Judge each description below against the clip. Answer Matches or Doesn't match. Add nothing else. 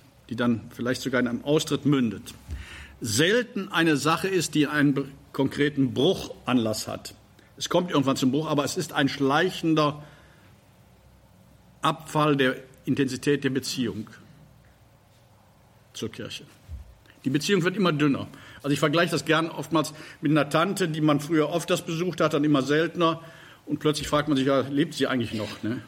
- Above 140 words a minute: Matches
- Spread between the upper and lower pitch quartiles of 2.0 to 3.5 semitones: Doesn't match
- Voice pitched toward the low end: Doesn't match